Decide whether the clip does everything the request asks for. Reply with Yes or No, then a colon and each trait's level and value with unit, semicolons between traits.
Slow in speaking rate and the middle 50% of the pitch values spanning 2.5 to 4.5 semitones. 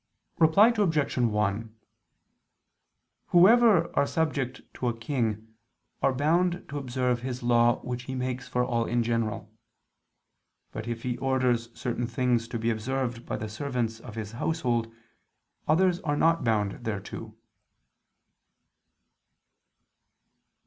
Yes: slow, 120 wpm; average, 3.7 semitones